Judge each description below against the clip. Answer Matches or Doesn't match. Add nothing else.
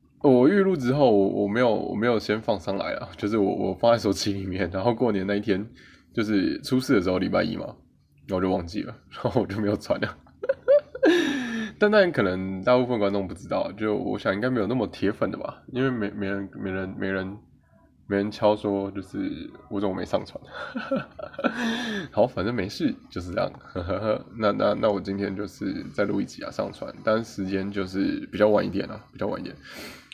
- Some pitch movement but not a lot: Matches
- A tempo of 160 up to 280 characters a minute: Doesn't match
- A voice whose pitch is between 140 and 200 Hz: Doesn't match